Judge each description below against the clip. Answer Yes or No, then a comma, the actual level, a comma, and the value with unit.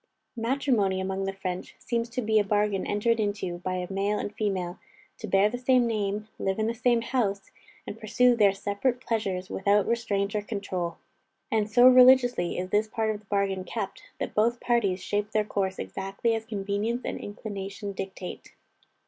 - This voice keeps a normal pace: Yes, average, 180 wpm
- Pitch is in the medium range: No, high, 205 Hz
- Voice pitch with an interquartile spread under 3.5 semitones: Yes, average, 2.9 semitones